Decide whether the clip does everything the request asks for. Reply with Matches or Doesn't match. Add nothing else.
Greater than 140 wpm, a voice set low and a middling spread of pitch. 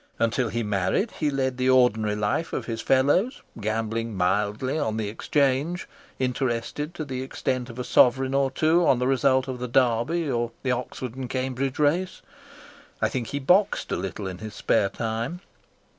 Matches